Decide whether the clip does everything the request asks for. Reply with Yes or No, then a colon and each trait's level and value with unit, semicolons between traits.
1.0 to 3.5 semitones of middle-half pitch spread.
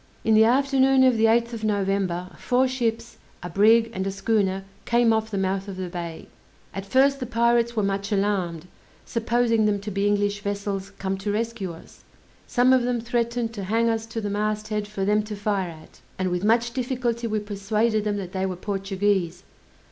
Yes: average, 2.9 semitones